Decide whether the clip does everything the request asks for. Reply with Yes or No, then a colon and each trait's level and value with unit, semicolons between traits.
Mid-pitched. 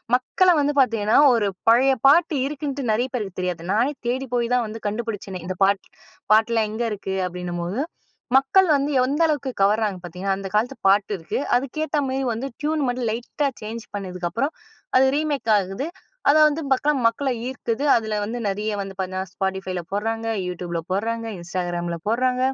No: high, 225 Hz